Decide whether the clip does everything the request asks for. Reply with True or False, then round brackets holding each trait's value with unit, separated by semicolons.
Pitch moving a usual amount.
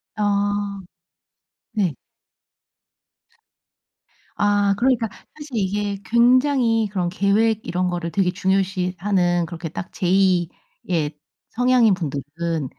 True (3.4 semitones)